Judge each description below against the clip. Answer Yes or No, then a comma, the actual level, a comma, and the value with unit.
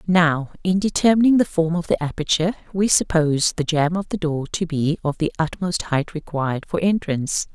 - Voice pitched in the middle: Yes, medium, 165 Hz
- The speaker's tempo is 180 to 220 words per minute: Yes, average, 190 wpm